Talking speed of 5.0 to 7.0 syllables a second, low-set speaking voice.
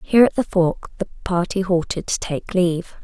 No: 5.3 syllables/s; medium, 185 Hz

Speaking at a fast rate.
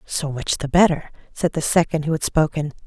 Yes: fast, 210 wpm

